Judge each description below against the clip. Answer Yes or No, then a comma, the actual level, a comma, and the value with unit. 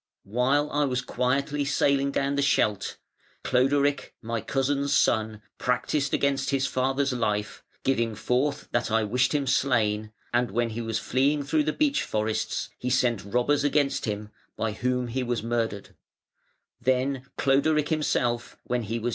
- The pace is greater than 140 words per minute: No, slow, 135 wpm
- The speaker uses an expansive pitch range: No, average, 3.8 semitones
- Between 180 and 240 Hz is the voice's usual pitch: No, low, 125 Hz